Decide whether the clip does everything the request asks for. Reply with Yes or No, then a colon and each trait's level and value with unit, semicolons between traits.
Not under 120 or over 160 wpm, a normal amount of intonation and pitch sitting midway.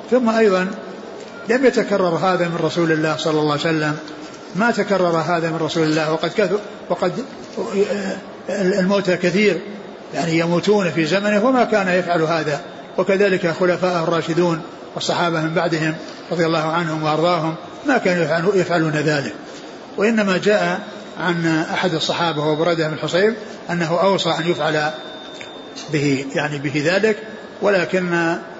Yes: average, 130 wpm; average, 3.5 semitones; medium, 175 Hz